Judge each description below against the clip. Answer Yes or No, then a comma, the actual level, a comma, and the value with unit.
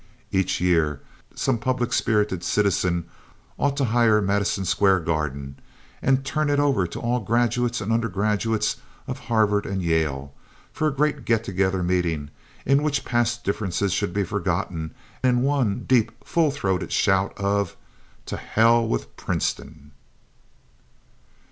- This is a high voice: No, low, 105 Hz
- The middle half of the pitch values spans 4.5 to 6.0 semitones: Yes, average, 5.2 semitones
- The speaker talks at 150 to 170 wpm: No, average, 140 wpm